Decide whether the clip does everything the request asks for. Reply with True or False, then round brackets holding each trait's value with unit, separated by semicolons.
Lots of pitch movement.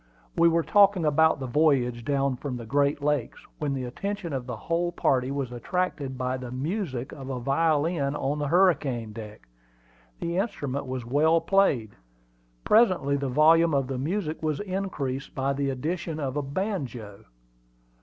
False (4.4 semitones)